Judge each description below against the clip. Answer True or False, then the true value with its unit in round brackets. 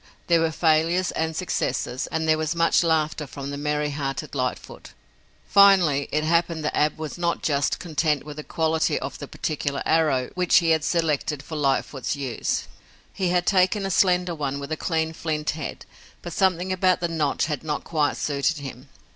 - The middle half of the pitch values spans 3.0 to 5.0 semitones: False (2.6 semitones)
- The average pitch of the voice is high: False (155 Hz)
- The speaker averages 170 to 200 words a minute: True (185 wpm)